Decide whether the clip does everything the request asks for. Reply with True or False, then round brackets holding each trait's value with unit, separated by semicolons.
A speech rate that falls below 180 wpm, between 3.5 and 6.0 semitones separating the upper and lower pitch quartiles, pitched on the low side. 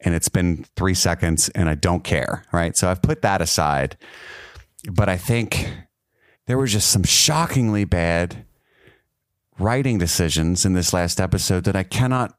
True (160 wpm; 5.1 semitones; 95 Hz)